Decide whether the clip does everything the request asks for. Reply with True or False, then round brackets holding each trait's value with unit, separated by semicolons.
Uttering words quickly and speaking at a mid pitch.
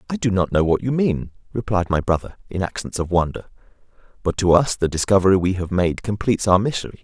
False (215 wpm; 95 Hz)